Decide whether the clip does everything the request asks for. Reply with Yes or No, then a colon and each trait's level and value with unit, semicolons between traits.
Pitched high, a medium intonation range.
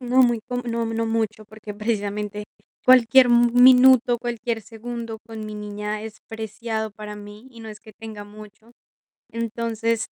No: high, 225 Hz; narrow, 1.9 semitones